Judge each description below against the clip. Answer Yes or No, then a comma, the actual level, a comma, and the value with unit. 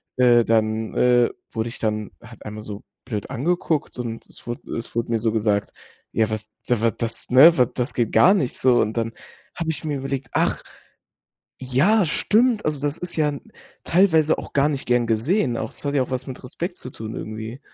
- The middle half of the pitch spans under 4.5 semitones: No, average, 4.9 semitones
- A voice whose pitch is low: Yes, low, 125 Hz